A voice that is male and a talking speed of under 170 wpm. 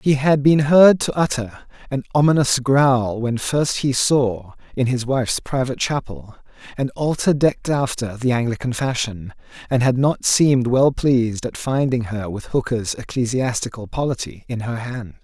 Yes: male; average, 160 wpm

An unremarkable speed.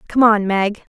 Yes: average, 190 wpm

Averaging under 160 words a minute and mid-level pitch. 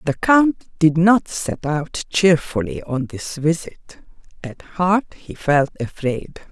Yes: average, 140 wpm; medium, 165 Hz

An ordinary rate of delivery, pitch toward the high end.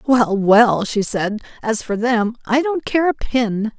Yes: average, 190 wpm; high, 230 Hz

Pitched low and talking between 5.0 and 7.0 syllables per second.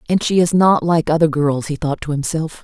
No: medium, 160 Hz; 5.3 syllables/s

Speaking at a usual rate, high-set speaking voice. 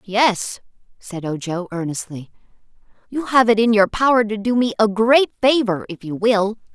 Yes: average, 170 wpm; high, 215 Hz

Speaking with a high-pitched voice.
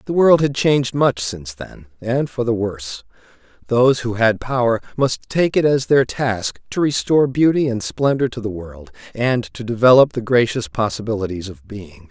No: low, 120 Hz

